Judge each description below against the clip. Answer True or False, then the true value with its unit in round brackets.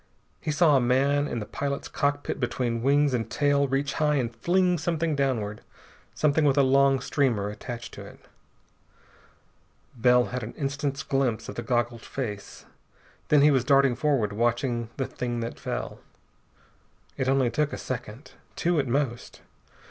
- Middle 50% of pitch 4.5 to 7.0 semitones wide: False (3.1 semitones)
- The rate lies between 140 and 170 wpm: True (160 wpm)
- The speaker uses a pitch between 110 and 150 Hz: True (135 Hz)